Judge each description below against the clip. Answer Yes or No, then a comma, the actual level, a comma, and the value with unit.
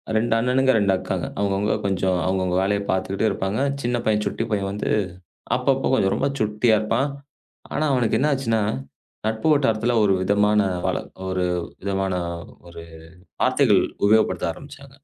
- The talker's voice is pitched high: No, low, 105 Hz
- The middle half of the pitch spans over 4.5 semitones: No, average, 3.4 semitones